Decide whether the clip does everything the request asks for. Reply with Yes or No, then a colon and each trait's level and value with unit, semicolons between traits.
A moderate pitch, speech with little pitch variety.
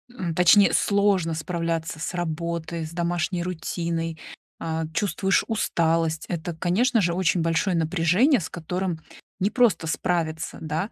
Yes: medium, 170 Hz; narrow, 2.2 semitones